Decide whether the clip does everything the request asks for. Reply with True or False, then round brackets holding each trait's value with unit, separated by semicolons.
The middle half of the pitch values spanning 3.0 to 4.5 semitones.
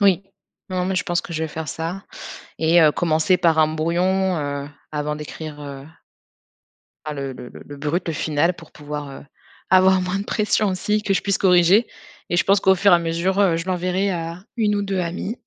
True (3.5 semitones)